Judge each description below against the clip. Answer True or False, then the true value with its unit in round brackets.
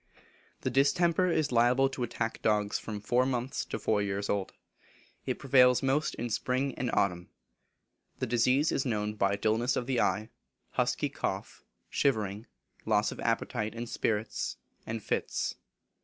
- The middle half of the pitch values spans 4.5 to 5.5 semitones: False (3.8 semitones)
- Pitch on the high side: False (120 Hz)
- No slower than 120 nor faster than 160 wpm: True (150 wpm)